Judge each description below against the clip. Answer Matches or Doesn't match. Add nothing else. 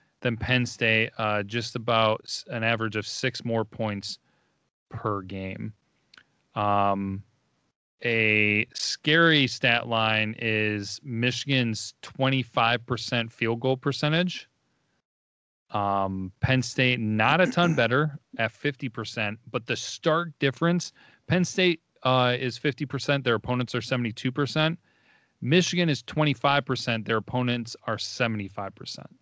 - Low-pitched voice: Matches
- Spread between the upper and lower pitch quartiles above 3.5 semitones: Matches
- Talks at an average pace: Doesn't match